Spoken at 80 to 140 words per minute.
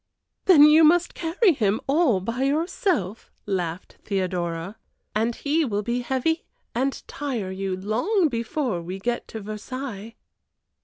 Yes: slow, 135 wpm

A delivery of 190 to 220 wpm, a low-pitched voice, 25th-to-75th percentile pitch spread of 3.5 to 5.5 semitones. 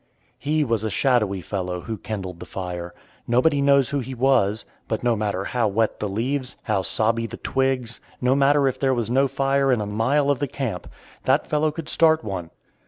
Yes: average, 200 wpm; low, 120 Hz; average, 4.7 semitones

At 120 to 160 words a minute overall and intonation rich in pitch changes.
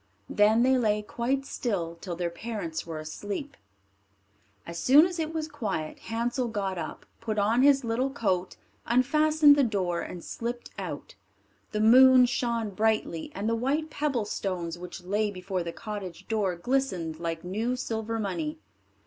Yes: average, 155 wpm; wide, 5.7 semitones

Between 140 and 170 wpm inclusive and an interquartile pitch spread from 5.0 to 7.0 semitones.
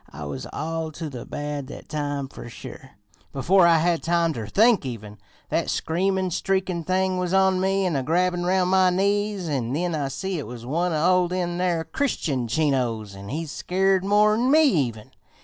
No: average, 185 wpm; average, 5.3 semitones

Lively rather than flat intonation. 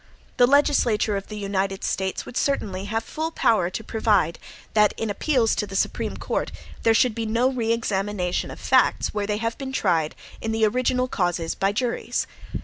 No: average, 3.3 semitones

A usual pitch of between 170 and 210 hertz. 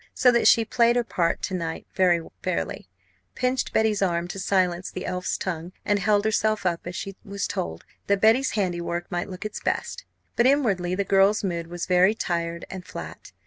Yes: high, 190 Hz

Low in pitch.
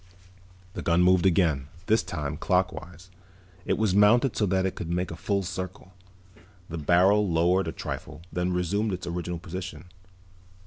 Yes: very low, 90 Hz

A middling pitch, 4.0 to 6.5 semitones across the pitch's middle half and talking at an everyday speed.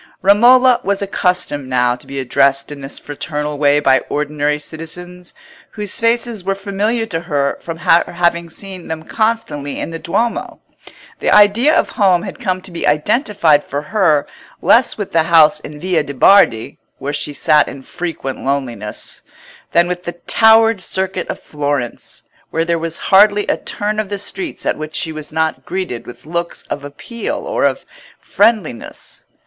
Yes: medium, 170 Hz; wide, 5.4 semitones; average, 170 wpm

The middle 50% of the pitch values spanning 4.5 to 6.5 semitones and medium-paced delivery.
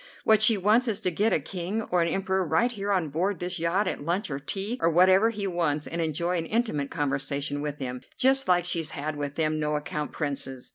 No: average, 5.0 semitones; fast, 230 wpm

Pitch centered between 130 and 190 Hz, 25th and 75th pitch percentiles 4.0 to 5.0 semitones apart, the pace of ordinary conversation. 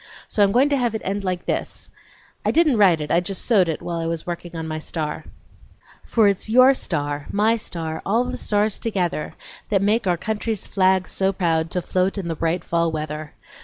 No: medium, 185 Hz; average, 4.3 semitones; fast, 210 wpm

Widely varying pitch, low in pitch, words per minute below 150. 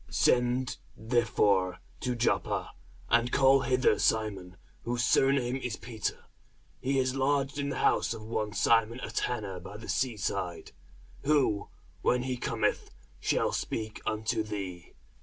No: average, 3.4 semitones; low, 115 Hz; average, 140 wpm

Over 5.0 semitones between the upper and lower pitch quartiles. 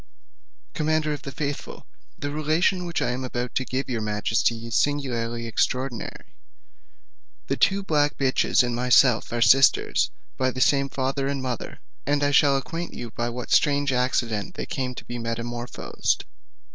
No: average, 3.2 semitones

